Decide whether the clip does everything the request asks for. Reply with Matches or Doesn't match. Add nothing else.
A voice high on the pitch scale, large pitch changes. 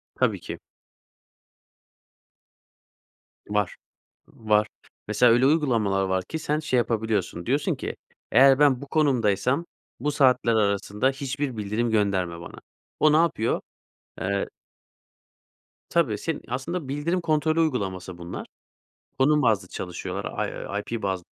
Doesn't match